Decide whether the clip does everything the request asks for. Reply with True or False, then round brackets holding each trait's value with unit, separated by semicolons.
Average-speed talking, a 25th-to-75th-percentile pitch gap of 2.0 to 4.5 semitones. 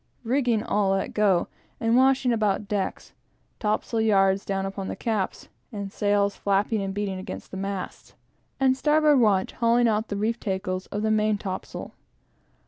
True (160 wpm; 2.8 semitones)